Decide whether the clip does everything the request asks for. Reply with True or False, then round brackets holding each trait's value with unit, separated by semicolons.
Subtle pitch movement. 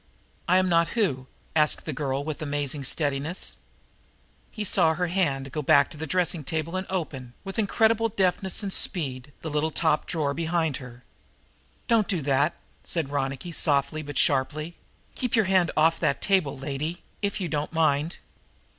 False (4.3 semitones)